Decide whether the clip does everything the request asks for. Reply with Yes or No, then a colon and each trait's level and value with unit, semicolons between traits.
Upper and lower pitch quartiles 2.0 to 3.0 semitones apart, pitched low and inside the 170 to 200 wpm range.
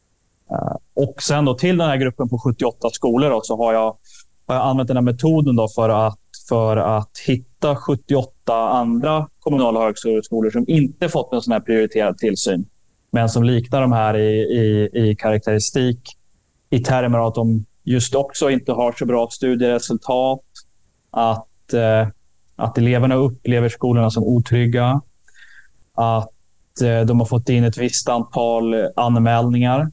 No: narrow, 2.5 semitones; low, 120 Hz; average, 150 wpm